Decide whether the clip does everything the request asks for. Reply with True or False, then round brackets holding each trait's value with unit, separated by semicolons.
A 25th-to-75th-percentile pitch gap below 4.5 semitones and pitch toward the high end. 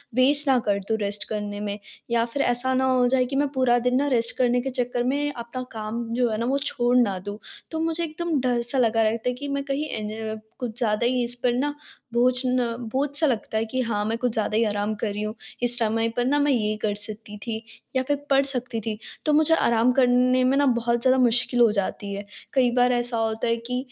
True (2.7 semitones; 245 Hz)